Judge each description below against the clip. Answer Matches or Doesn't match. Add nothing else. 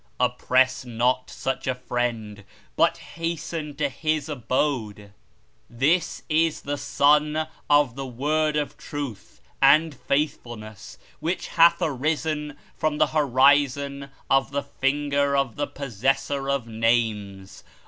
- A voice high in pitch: Doesn't match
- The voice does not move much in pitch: Doesn't match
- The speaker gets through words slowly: Matches